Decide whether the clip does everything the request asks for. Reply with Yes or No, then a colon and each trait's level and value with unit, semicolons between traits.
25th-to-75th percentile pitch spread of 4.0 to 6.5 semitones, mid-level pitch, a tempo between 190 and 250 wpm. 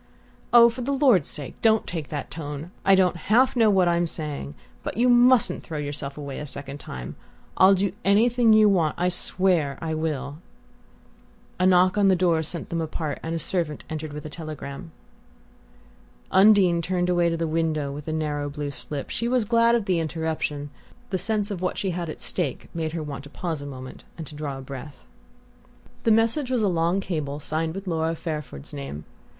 Yes: average, 4.6 semitones; medium, 165 Hz; average, 195 wpm